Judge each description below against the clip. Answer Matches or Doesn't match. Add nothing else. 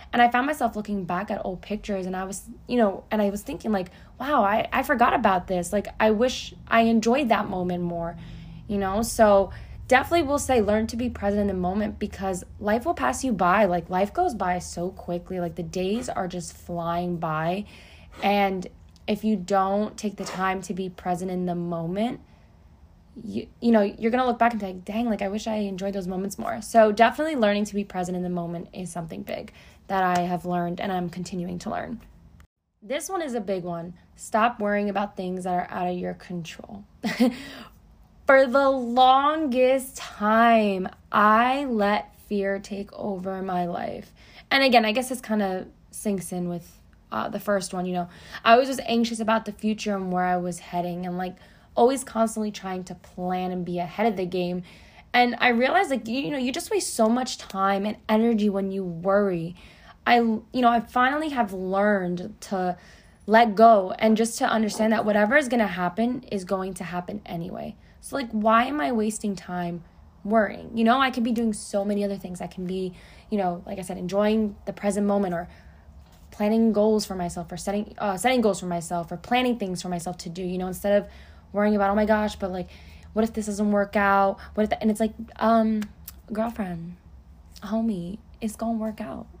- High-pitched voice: Matches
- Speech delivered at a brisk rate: Matches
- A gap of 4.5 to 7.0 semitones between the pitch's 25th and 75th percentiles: Doesn't match